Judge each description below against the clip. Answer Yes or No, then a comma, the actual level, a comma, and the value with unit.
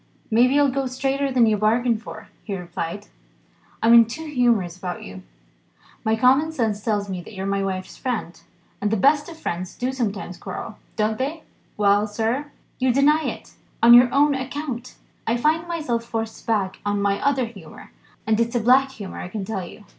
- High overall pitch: Yes, high, 230 Hz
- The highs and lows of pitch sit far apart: No, average, 4.6 semitones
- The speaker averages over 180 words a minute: Yes, average, 190 wpm